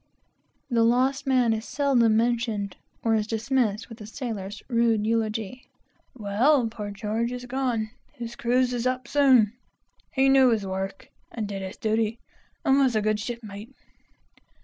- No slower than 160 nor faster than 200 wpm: No, average, 150 wpm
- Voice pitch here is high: Yes, high, 230 Hz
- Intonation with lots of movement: No, average, 2.8 semitones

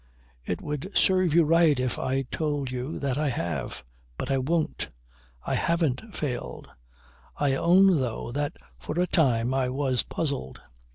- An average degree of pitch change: Yes, average, 4.3 semitones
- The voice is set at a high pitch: No, medium, 140 Hz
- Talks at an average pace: Yes, average, 155 wpm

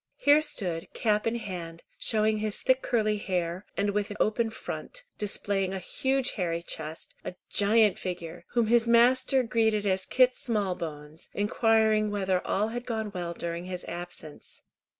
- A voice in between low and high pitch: No, high, 210 Hz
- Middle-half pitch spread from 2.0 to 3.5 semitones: No, average, 4.2 semitones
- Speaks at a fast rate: No, average, 150 wpm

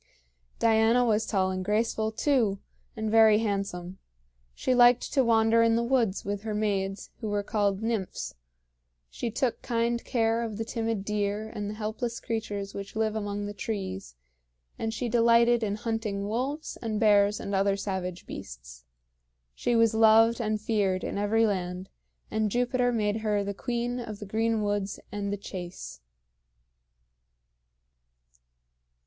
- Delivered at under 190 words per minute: Yes, average, 150 wpm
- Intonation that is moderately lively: No, narrow, 2.2 semitones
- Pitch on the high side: Yes, high, 215 Hz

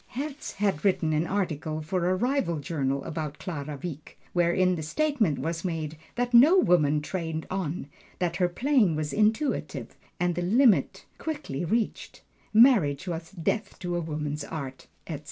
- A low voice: No, medium, 175 Hz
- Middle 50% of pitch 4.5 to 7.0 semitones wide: Yes, average, 5.3 semitones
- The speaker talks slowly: No, average, 155 wpm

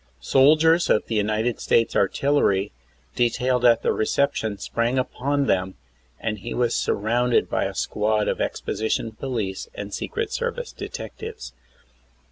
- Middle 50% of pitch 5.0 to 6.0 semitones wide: No, average, 3.3 semitones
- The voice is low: Yes, low, 115 Hz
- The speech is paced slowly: Yes, slow, 125 wpm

